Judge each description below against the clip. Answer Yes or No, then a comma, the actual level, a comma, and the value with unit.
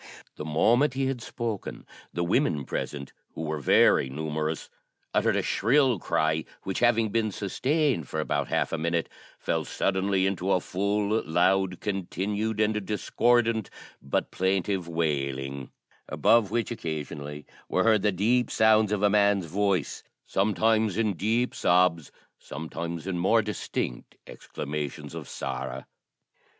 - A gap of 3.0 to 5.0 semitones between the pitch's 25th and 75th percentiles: No, wide, 5.5 semitones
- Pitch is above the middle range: No, very low, 95 Hz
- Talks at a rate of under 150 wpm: Yes, slow, 135 wpm